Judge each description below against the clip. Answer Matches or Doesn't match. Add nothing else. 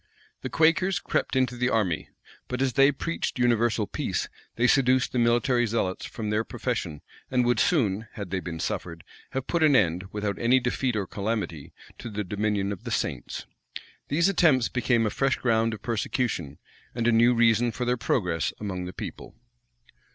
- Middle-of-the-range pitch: Doesn't match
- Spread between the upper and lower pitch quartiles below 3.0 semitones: Doesn't match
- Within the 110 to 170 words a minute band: Doesn't match